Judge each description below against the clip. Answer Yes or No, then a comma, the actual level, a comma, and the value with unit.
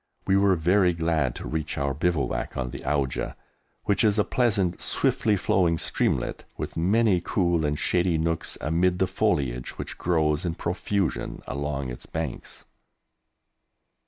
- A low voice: Yes, very low, 85 Hz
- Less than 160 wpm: Yes, average, 145 wpm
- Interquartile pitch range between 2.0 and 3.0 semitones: No, average, 4.0 semitones